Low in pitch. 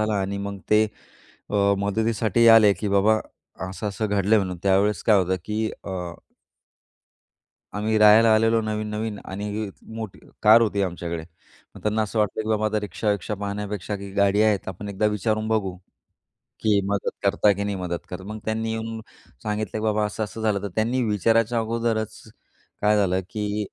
Yes: low, 105 Hz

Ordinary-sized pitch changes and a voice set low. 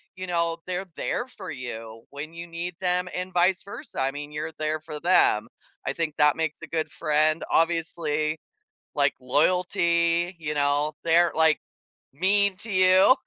No: average, 3.2 semitones; medium, 165 Hz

